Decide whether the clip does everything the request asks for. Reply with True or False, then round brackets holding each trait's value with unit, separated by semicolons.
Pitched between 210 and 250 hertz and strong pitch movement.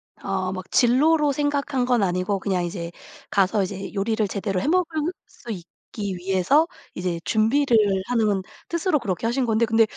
True (220 Hz; 6.2 semitones)